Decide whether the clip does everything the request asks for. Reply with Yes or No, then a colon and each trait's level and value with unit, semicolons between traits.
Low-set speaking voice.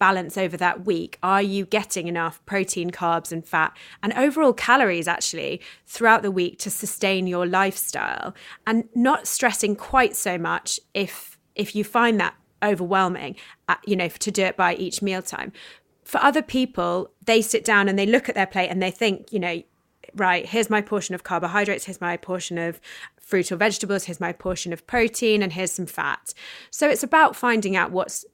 No: high, 195 Hz